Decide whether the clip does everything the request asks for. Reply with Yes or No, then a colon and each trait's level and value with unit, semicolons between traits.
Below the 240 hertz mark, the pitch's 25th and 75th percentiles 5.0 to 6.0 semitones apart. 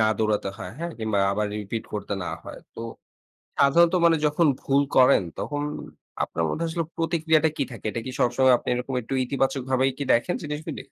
Yes: low, 135 Hz; wide, 5.5 semitones